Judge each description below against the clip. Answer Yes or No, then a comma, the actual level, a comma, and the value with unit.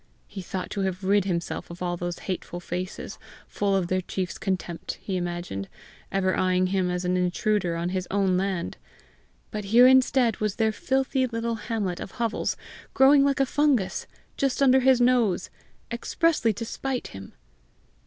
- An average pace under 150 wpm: No, average, 165 wpm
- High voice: Yes, high, 195 Hz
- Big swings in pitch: No, average, 4.8 semitones